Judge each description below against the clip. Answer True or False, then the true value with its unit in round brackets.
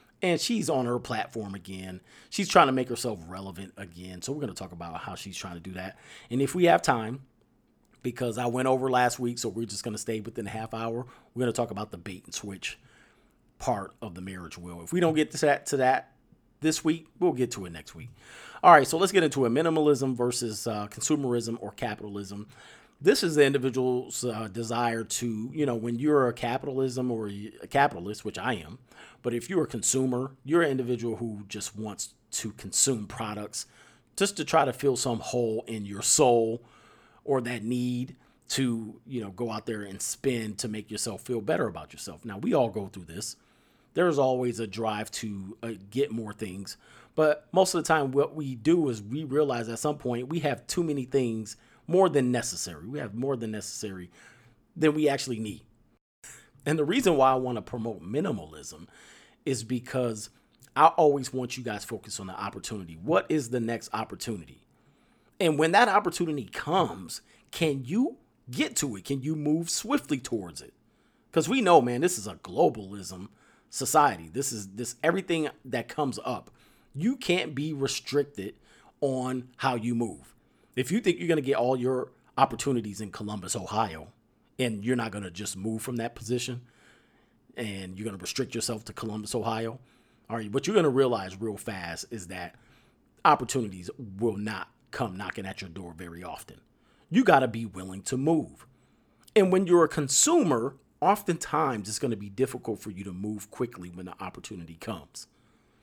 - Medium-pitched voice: False (120 Hz)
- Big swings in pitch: False (4.2 semitones)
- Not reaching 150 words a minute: False (195 wpm)